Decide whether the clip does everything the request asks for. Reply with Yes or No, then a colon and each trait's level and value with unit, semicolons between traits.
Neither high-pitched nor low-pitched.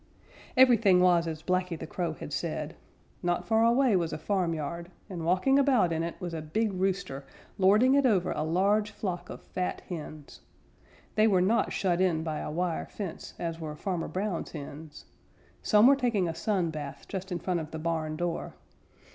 Yes: medium, 180 Hz